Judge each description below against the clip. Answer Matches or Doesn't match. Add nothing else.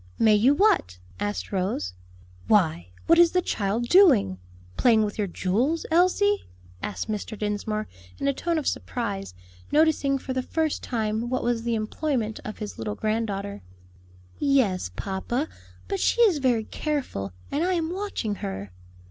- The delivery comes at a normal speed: Matches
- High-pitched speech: Matches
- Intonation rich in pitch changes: Matches